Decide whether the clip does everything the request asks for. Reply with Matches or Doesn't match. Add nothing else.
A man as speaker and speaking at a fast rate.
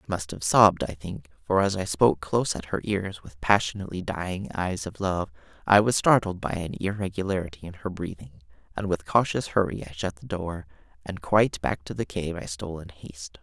Matches